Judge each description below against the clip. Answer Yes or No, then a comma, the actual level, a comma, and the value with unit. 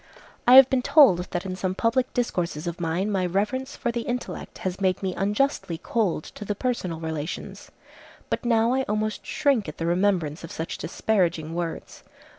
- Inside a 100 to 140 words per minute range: No, average, 180 wpm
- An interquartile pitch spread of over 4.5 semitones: Yes, wide, 5.6 semitones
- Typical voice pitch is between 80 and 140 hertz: No, high, 195 Hz